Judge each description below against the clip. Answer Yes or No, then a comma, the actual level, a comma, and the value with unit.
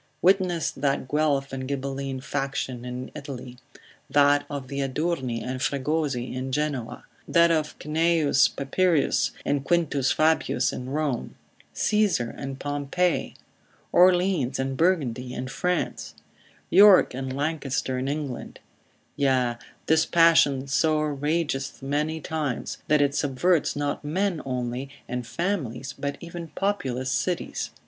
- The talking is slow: Yes, slow, 120 wpm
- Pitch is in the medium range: Yes, medium, 145 Hz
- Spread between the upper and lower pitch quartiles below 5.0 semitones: Yes, average, 3.5 semitones